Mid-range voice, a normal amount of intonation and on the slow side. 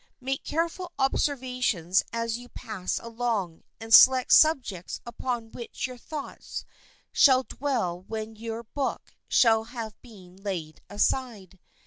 No: high, 230 Hz; average, 4.0 semitones; slow, 120 wpm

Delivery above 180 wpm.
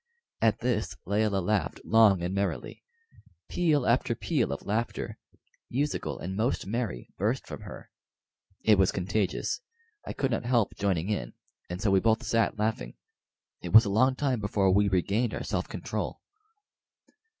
No: average, 155 wpm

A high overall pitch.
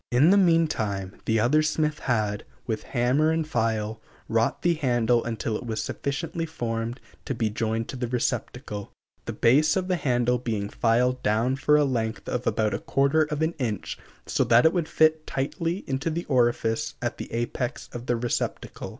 No: low, 125 Hz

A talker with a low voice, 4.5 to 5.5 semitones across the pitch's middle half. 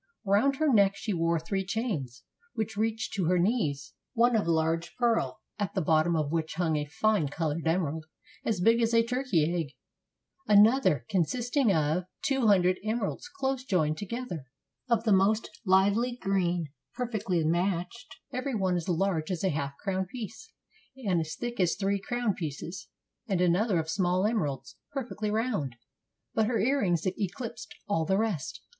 No: high, 195 Hz; average, 5.2 semitones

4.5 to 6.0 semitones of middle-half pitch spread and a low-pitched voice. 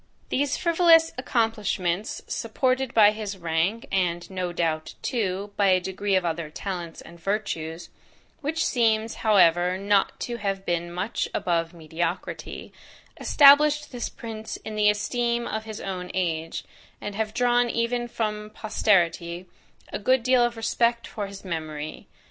No: average, 5.1 semitones; high, 205 Hz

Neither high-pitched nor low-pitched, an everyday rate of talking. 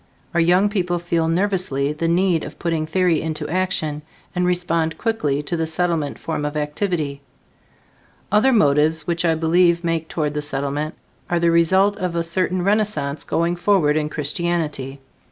Yes: medium, 165 Hz; average, 160 wpm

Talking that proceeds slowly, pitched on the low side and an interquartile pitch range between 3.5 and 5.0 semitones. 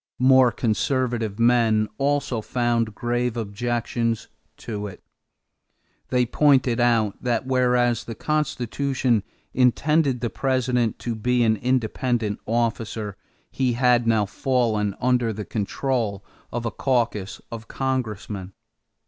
No: slow, 115 wpm; low, 120 Hz; narrow, 2.4 semitones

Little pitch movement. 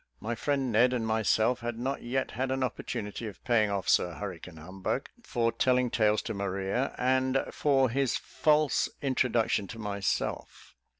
No: average, 3.9 semitones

